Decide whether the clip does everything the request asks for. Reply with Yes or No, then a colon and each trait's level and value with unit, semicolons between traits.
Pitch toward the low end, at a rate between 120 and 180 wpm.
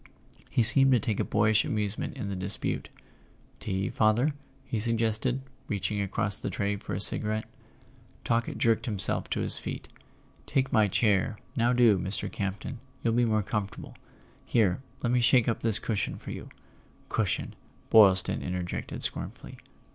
Yes: low, 110 Hz; average, 160 wpm